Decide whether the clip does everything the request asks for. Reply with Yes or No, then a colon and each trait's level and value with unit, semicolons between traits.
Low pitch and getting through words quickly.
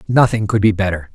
Yes: low, 105 Hz; fast, 210 wpm